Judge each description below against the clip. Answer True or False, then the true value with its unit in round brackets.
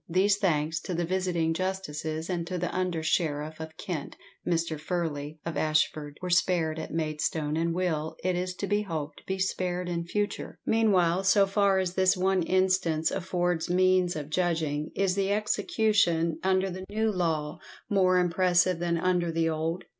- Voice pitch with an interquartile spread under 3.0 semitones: True (2.6 semitones)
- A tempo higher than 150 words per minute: True (170 wpm)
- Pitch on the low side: False (175 Hz)